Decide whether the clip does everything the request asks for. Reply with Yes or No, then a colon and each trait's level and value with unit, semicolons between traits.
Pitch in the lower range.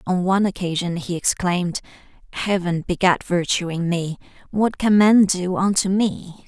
No: medium, 185 Hz